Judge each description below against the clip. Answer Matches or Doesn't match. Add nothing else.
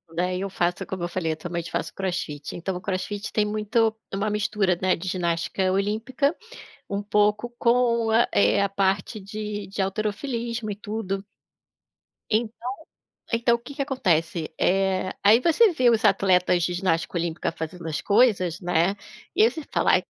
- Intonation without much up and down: Doesn't match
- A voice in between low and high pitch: Doesn't match